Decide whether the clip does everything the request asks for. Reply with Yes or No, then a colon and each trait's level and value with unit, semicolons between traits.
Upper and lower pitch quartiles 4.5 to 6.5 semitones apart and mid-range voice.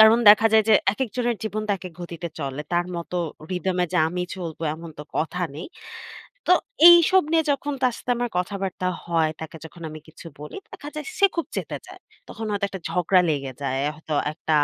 Yes: wide, 5.4 semitones; medium, 180 Hz